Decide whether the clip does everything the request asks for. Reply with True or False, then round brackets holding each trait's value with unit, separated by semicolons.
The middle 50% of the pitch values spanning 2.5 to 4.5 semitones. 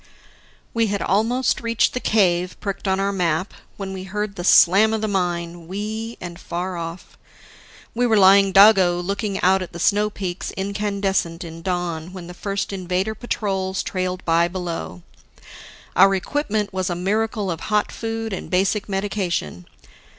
True (2.8 semitones)